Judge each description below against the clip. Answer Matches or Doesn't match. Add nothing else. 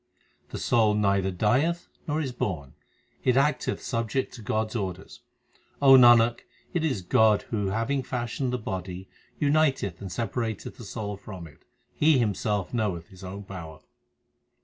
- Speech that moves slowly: Doesn't match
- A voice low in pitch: Matches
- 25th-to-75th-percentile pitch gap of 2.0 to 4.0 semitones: Doesn't match